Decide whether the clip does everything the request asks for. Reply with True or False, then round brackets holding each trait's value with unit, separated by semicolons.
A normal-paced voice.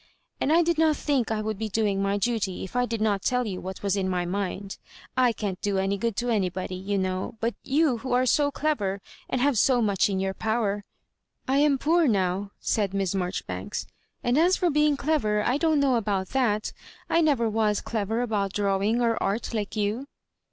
False (215 wpm)